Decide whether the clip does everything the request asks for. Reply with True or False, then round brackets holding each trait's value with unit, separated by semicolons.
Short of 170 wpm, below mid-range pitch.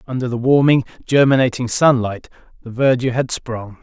True (140 wpm; 125 Hz)